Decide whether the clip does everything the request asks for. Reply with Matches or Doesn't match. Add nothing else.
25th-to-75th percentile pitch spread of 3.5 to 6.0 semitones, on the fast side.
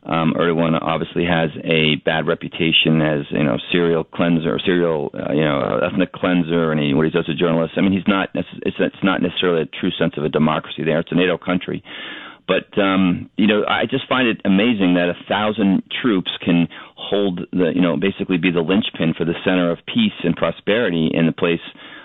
Doesn't match